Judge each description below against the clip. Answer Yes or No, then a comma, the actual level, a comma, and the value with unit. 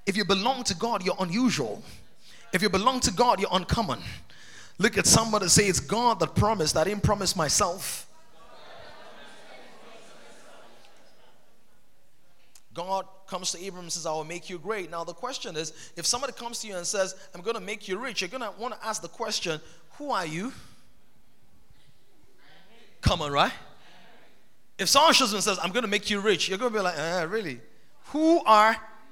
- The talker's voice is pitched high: Yes, high, 200 Hz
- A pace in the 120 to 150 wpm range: No, average, 185 wpm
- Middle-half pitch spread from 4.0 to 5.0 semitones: Yes, average, 4.5 semitones